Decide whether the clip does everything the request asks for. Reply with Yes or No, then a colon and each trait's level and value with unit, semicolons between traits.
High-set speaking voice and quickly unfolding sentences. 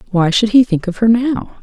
Yes: high, 210 Hz; fast, 260 wpm